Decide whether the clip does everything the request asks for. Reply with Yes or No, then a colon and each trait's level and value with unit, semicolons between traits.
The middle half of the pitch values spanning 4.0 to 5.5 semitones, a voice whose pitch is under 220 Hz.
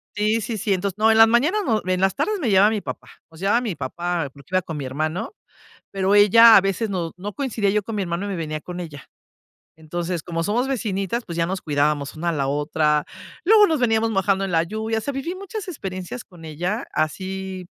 Yes: average, 4.9 semitones; high, 190 Hz